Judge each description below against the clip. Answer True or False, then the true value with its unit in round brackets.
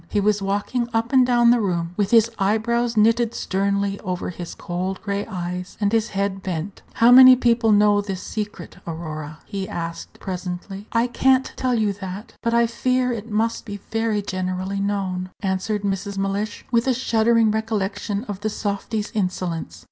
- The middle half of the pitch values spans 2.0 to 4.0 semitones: True (3.2 semitones)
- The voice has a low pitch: False (205 Hz)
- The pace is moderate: True (170 wpm)